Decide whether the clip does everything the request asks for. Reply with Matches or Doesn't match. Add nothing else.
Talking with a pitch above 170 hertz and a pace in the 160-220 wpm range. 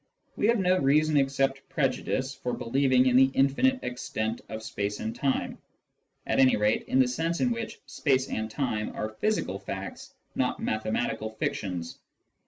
Doesn't match